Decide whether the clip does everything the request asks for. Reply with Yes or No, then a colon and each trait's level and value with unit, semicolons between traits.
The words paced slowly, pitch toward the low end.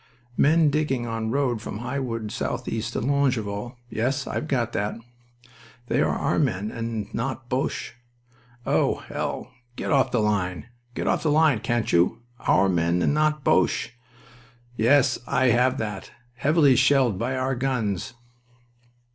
No: average, 145 wpm; low, 120 Hz